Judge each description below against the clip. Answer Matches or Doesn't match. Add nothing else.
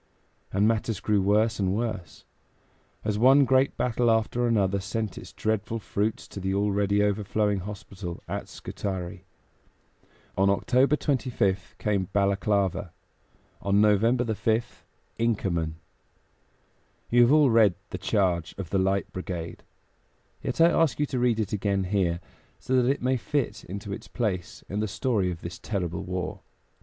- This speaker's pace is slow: Doesn't match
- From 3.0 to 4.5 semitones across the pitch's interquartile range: Matches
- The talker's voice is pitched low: Matches